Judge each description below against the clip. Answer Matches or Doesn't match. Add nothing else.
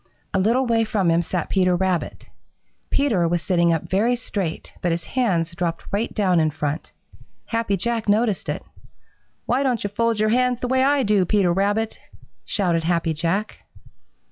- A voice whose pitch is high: Matches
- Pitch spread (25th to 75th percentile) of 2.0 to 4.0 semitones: Doesn't match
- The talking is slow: Doesn't match